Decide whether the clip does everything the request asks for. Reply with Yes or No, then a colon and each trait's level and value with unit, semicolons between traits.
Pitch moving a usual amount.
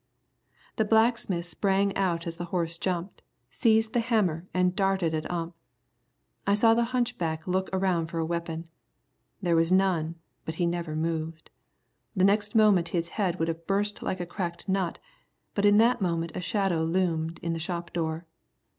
Yes: average, 3.1 semitones